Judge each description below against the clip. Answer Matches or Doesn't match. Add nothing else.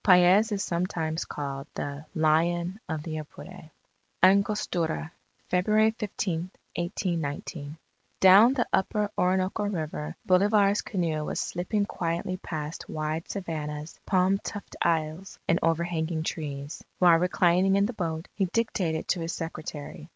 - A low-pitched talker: Doesn't match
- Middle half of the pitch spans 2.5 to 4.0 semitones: Matches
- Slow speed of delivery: Matches